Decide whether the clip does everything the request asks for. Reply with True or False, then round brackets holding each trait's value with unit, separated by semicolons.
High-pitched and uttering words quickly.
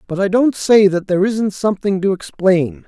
True (195 Hz; 210 wpm)